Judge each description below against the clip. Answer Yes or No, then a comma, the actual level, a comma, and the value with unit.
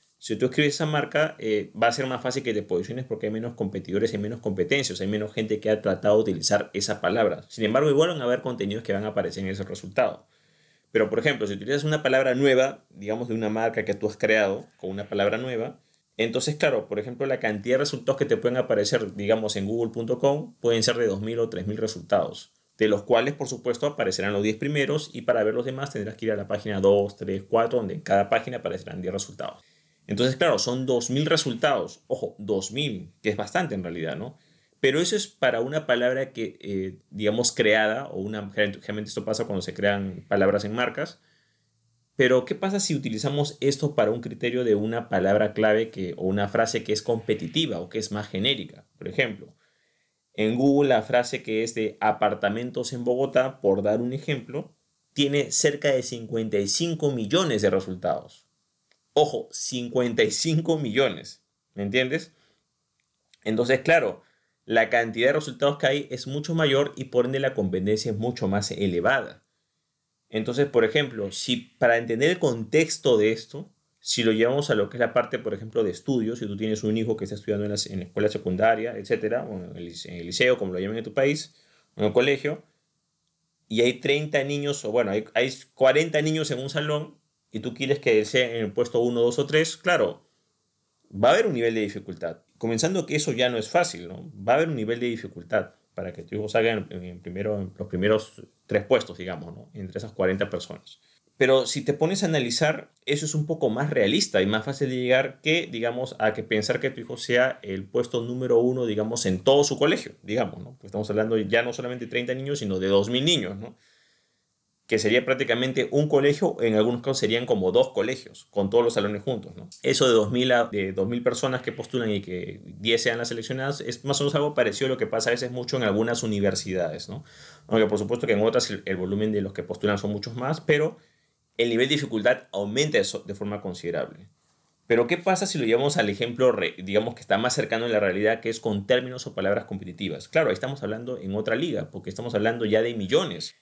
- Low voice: Yes, low, 120 Hz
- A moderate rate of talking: No, fast, 215 wpm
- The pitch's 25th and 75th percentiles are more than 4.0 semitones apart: Yes, average, 4.7 semitones